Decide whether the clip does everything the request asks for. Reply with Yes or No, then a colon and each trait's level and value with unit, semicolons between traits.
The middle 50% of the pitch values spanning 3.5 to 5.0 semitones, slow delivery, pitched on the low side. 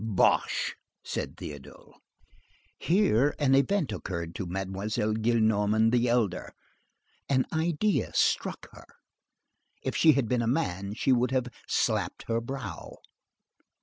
Yes: average, 4.6 semitones; slow, 115 wpm; low, 120 Hz